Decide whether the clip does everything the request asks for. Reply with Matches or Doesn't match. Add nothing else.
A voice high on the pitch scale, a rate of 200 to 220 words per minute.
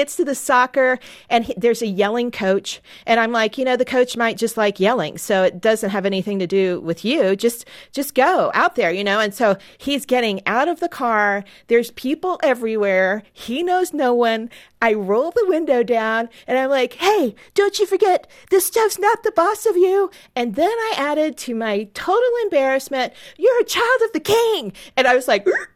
Matches